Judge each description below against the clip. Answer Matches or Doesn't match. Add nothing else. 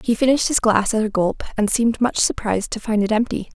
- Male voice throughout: Doesn't match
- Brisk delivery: Matches